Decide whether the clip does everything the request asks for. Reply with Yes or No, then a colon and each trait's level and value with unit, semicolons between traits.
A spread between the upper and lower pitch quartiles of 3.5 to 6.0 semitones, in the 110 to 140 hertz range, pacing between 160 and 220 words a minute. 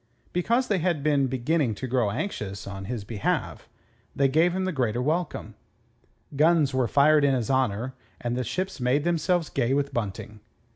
Yes: average, 5.3 semitones; low, 135 Hz; average, 175 wpm